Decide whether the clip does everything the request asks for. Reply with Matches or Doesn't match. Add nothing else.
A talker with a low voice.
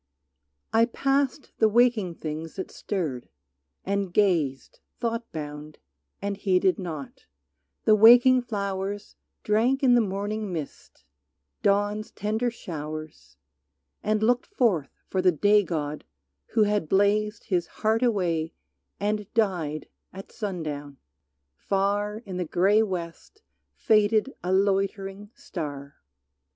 Doesn't match